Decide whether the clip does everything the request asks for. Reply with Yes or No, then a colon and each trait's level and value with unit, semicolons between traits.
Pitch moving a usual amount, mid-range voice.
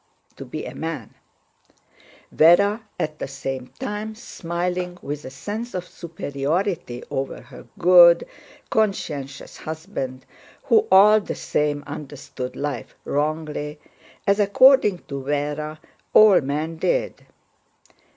No: wide, 5.7 semitones; medium, 160 Hz